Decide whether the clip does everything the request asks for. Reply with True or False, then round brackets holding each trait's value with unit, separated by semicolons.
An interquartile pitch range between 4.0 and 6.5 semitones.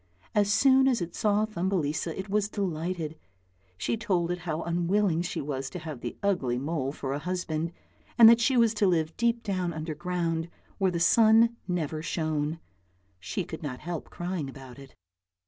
True (4.5 semitones)